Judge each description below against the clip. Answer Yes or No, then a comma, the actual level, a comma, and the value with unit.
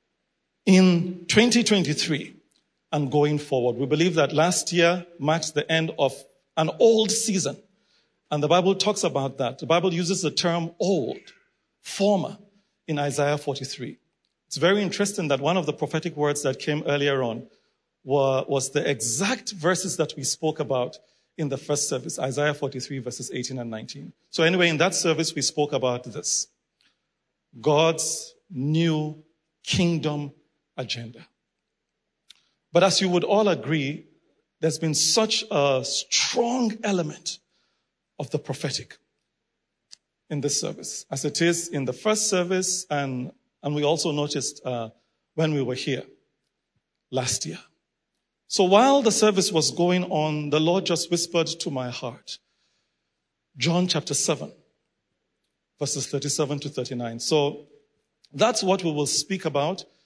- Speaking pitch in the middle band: Yes, medium, 155 Hz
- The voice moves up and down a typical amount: Yes, average, 4.3 semitones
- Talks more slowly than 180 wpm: Yes, average, 145 wpm